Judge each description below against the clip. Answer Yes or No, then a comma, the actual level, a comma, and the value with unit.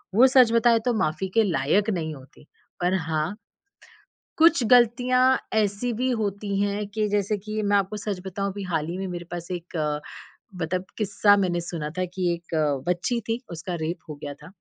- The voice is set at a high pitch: Yes, high, 195 Hz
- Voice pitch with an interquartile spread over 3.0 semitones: Yes, average, 3.9 semitones